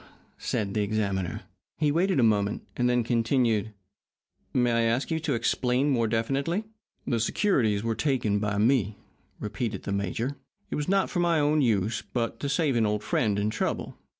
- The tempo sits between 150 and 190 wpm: Yes, average, 180 wpm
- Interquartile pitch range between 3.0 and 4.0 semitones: No, average, 4.7 semitones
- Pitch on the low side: Yes, low, 115 Hz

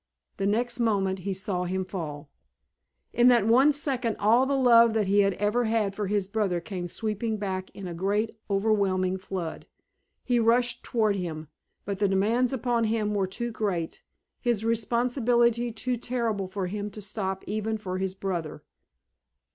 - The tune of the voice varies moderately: Yes, average, 3.5 semitones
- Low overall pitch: No, high, 210 Hz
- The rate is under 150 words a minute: No, average, 165 wpm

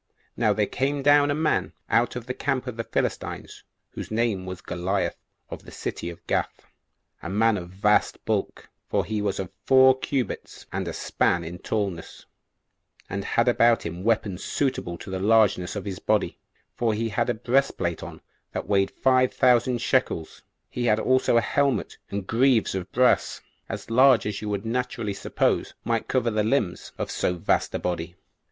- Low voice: Yes, low, 110 Hz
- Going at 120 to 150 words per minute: No, average, 180 wpm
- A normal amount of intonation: Yes, average, 4.6 semitones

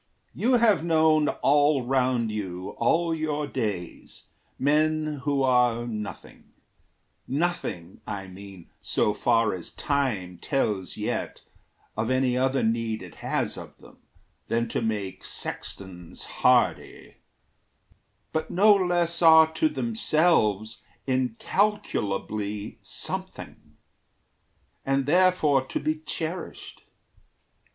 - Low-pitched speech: Yes, low, 130 Hz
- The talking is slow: Yes, slow, 105 wpm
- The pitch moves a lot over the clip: Yes, wide, 6.7 semitones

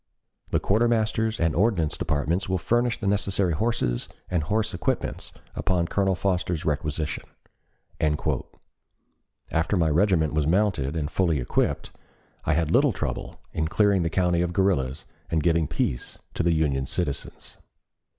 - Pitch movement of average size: Yes, average, 4.2 semitones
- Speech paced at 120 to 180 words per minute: Yes, average, 140 wpm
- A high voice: No, very low, 85 Hz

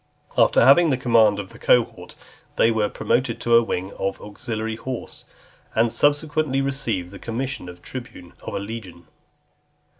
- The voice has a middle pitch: No, low, 115 Hz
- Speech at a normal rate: Yes, average, 155 wpm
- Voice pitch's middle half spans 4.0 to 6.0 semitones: Yes, average, 4.3 semitones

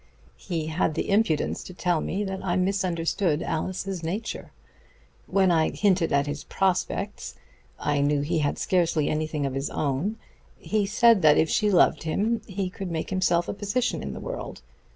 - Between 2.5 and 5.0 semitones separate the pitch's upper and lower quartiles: Yes, average, 4.0 semitones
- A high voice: No, medium, 180 Hz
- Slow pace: No, average, 175 wpm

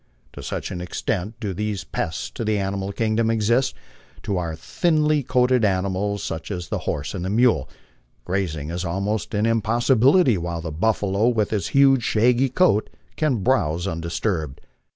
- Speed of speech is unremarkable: Yes, average, 160 wpm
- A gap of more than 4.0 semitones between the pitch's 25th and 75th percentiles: Yes, average, 5.0 semitones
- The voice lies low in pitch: Yes, low, 105 Hz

